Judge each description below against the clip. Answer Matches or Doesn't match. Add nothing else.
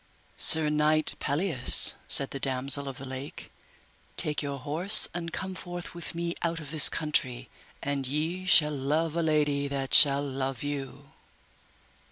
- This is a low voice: Doesn't match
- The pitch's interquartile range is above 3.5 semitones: Doesn't match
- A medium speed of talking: Matches